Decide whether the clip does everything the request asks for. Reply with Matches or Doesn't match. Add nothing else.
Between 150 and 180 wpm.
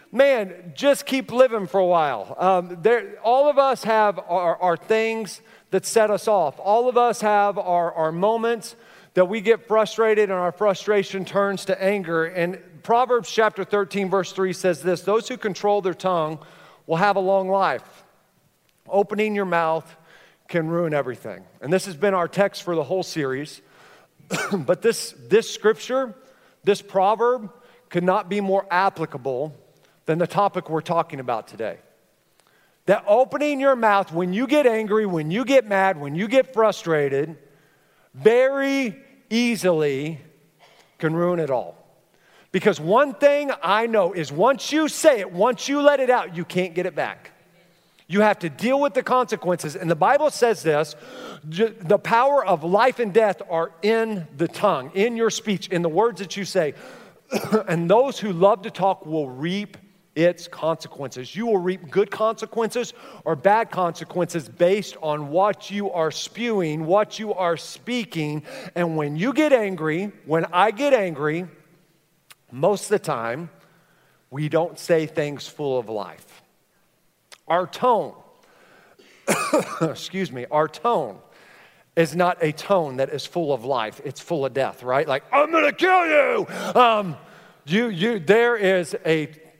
Matches